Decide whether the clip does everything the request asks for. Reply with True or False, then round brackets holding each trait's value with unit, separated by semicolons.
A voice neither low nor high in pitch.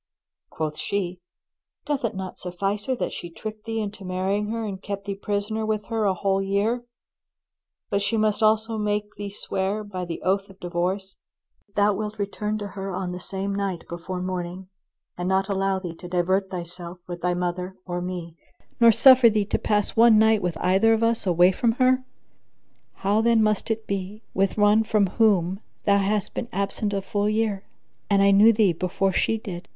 False (200 Hz)